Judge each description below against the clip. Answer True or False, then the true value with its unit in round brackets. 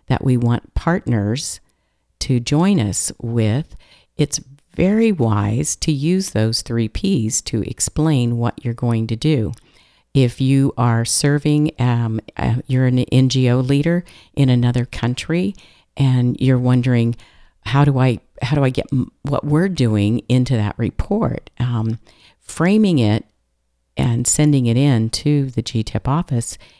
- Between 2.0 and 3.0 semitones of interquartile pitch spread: False (4.0 semitones)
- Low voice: True (125 Hz)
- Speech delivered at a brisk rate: False (145 wpm)